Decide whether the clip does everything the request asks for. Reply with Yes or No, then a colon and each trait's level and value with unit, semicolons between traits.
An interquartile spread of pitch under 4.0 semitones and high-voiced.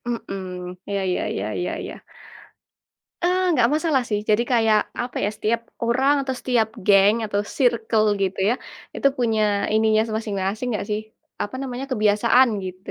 Yes: average, 3.2 semitones; high, 220 Hz